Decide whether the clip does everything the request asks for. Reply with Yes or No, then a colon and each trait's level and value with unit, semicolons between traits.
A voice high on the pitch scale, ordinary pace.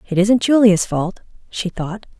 Yes: high, 200 Hz; average, 165 wpm